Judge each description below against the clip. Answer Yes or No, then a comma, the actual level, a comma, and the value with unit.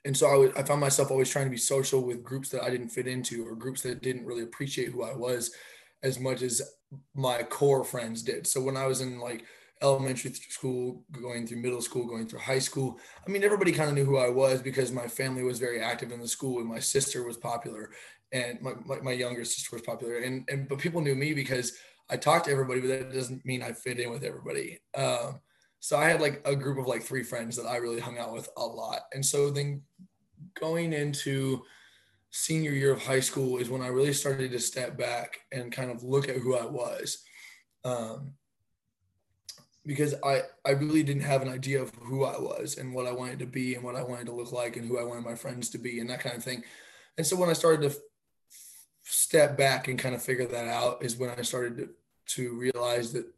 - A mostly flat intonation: Yes, narrow, 2.2 semitones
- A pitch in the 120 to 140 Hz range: Yes, low, 130 Hz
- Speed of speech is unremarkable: No, fast, 235 wpm